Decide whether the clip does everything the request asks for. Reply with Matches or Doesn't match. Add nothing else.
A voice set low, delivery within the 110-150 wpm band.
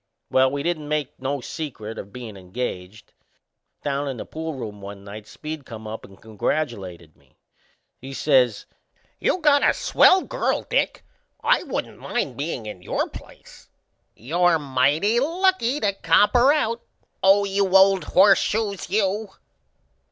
Doesn't match